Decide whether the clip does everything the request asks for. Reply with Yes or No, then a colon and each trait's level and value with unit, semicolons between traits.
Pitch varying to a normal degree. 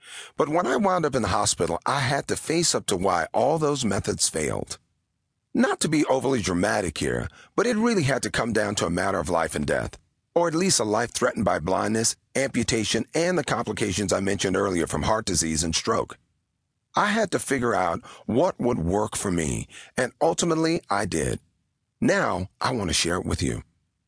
No: wide, 7.3 semitones